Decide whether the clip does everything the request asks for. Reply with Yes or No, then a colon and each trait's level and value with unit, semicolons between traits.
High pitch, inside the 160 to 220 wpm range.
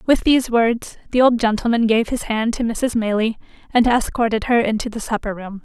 Yes: high, 230 Hz; average, 200 wpm